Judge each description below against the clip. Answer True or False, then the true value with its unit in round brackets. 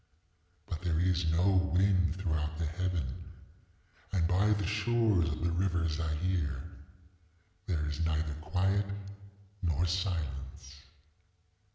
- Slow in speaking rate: True (110 wpm)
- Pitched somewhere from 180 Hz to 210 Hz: False (85 Hz)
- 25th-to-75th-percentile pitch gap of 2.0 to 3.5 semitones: True (2.9 semitones)